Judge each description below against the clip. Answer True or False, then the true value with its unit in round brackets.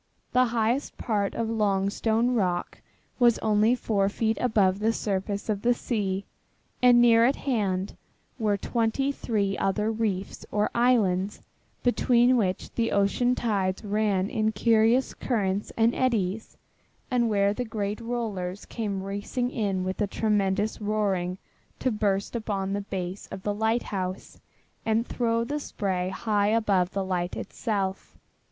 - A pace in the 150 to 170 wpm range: False (140 wpm)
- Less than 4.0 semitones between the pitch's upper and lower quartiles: True (2.9 semitones)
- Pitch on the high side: True (210 Hz)